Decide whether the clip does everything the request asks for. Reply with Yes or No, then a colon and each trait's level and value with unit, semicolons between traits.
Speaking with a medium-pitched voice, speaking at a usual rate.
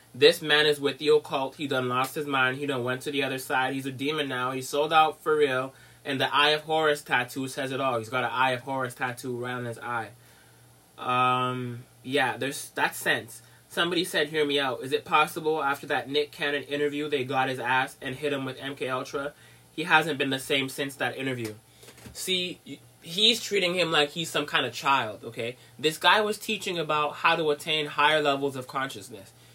No: medium, 145 Hz; fast, 215 wpm